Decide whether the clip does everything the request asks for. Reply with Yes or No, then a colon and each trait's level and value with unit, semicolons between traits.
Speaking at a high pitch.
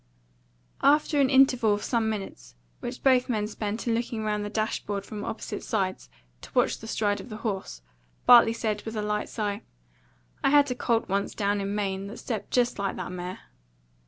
Yes: high, 215 Hz